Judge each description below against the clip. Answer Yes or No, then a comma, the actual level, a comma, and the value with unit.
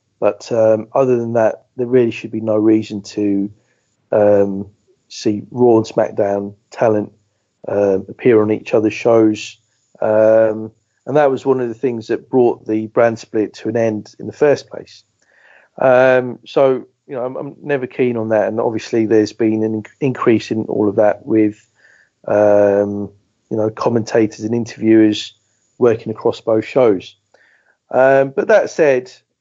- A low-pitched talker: Yes, low, 110 Hz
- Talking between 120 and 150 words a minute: No, average, 160 wpm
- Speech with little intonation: Yes, narrow, 1.9 semitones